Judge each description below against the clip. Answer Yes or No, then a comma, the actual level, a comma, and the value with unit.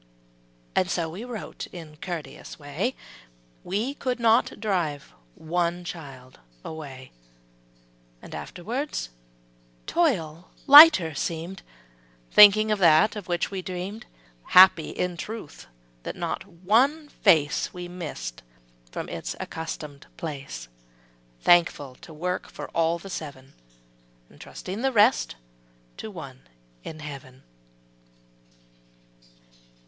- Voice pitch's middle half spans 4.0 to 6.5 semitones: Yes, wide, 5.4 semitones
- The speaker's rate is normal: No, slow, 110 wpm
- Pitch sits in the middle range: Yes, medium, 175 Hz